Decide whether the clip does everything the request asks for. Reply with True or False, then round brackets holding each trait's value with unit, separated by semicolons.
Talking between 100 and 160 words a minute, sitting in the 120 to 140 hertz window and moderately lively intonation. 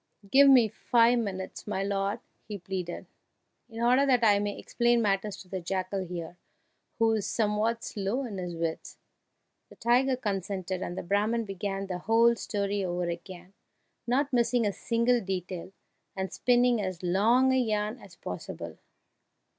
False (155 wpm; 205 Hz; 3.9 semitones)